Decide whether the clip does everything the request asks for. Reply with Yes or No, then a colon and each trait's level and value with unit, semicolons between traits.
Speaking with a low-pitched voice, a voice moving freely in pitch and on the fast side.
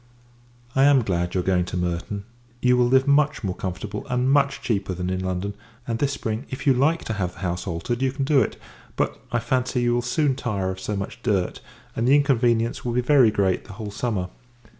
Yes: low, 115 Hz; wide, 5.7 semitones; fast, 225 wpm